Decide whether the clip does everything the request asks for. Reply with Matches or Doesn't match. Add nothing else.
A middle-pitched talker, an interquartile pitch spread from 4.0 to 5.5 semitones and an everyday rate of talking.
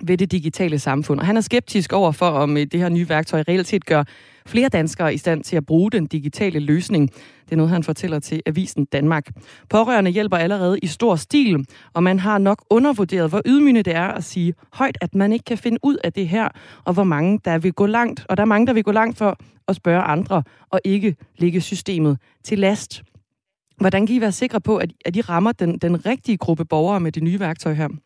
Doesn't match